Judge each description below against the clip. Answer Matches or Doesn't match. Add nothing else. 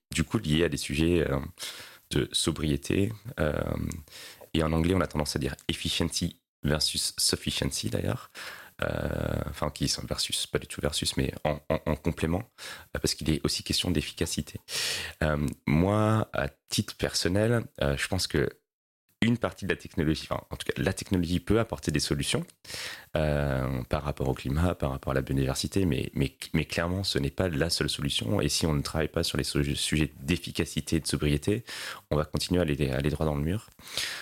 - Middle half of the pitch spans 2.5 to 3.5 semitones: Matches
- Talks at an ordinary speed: Matches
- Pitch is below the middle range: Matches